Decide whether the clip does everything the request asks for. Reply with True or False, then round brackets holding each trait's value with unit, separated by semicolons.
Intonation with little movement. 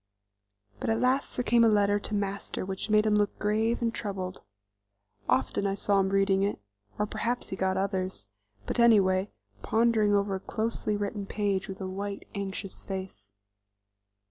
True (2.0 semitones)